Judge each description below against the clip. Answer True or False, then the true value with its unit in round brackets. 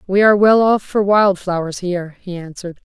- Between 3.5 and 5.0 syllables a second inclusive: False (5.6 syllables/s)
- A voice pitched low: False (190 Hz)